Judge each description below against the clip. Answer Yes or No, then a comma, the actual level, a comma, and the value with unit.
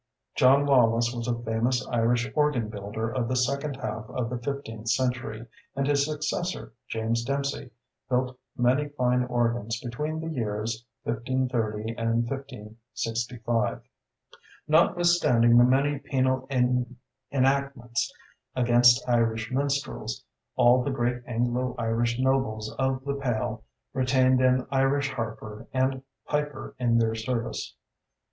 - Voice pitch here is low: Yes, low, 125 Hz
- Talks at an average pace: No, slow, 120 wpm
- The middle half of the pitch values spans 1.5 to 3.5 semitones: Yes, average, 2.7 semitones